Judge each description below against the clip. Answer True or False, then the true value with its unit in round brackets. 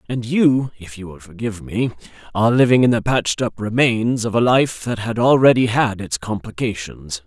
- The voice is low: True (115 Hz)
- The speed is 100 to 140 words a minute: False (175 wpm)